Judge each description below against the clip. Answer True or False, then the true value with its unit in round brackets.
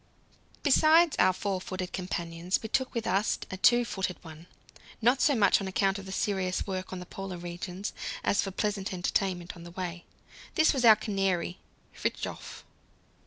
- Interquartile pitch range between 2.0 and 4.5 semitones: True (2.8 semitones)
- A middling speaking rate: True (170 wpm)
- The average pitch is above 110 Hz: True (190 Hz)